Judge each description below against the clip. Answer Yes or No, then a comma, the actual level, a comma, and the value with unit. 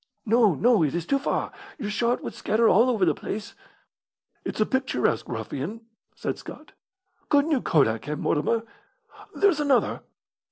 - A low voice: No, high, 220 Hz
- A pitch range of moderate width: No, wide, 8.2 semitones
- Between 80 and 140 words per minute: No, average, 155 wpm